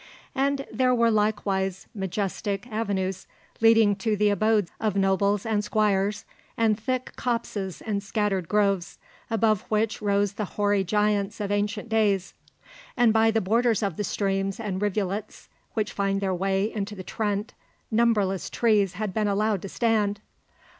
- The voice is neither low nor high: No, high, 210 Hz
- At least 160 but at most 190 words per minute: No, average, 150 wpm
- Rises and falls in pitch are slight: Yes, narrow, 2.0 semitones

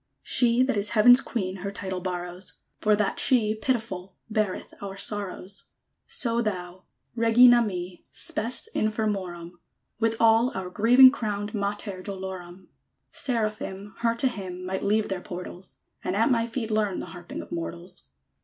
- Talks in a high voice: Yes, high, 205 Hz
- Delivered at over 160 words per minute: No, average, 150 wpm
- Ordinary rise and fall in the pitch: Yes, average, 3.6 semitones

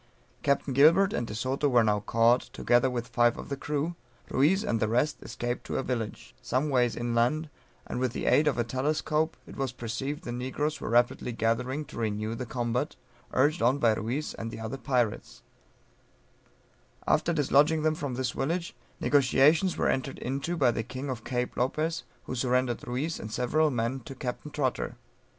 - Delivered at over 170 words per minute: Yes, average, 180 wpm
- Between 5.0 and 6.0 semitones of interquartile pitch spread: No, average, 3.7 semitones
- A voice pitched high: No, low, 130 Hz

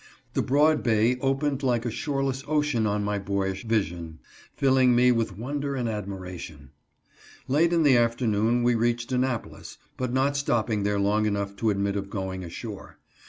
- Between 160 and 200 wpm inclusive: Yes, average, 165 wpm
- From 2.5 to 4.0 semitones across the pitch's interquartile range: No, average, 4.6 semitones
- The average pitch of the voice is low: Yes, low, 115 Hz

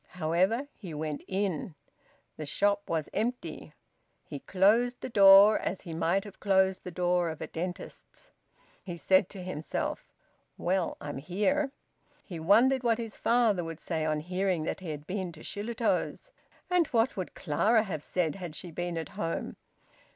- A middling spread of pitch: Yes, average, 4.3 semitones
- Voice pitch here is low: No, medium, 185 Hz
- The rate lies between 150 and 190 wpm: Yes, average, 165 wpm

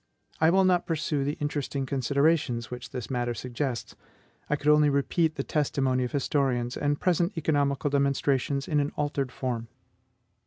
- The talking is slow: No, average, 155 wpm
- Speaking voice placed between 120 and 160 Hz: Yes, medium, 140 Hz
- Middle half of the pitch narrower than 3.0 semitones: Yes, narrow, 2.6 semitones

